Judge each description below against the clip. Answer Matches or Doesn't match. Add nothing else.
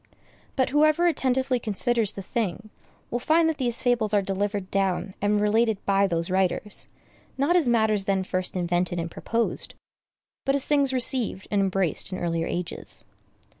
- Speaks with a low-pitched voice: Doesn't match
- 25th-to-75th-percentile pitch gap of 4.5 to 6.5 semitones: Matches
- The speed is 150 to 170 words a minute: Matches